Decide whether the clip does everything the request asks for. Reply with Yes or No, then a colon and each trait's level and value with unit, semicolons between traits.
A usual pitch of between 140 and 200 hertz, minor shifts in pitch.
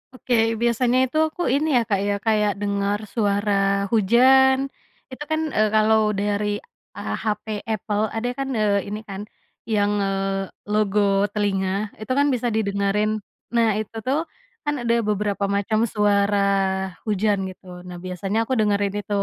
No: high, 210 Hz; narrow, 2.1 semitones